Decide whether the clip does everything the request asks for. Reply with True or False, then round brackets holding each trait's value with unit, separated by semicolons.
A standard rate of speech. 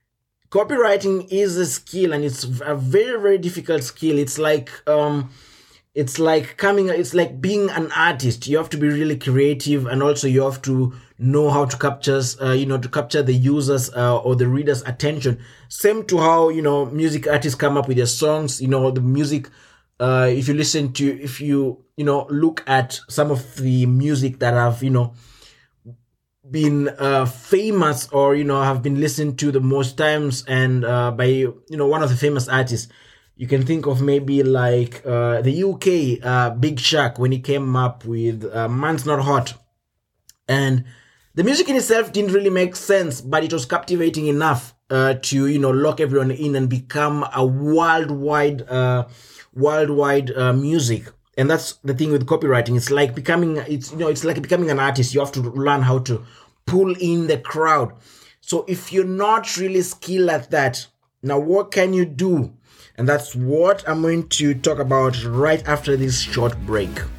True (190 wpm)